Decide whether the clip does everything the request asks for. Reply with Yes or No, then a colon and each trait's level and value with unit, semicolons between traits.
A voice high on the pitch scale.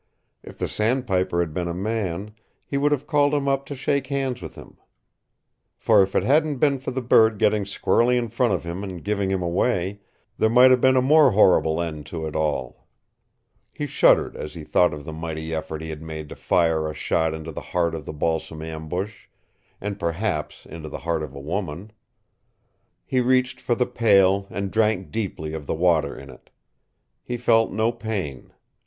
No: very low, 95 Hz